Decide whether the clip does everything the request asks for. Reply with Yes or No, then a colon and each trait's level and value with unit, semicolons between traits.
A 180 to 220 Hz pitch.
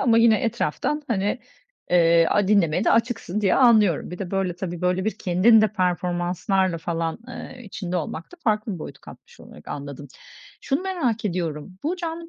Yes: high, 190 Hz